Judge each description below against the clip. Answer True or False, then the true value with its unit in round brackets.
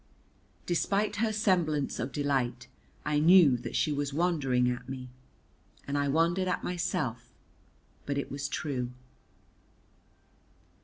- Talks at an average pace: False (120 wpm)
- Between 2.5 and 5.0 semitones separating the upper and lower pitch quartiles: True (4.6 semitones)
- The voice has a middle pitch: True (145 Hz)